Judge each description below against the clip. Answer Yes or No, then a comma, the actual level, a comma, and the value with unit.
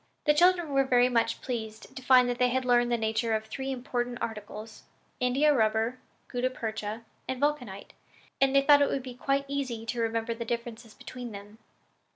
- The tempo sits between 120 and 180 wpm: No, average, 190 wpm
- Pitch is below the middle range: No, high, 245 Hz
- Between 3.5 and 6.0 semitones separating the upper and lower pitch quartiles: No, average, 2.9 semitones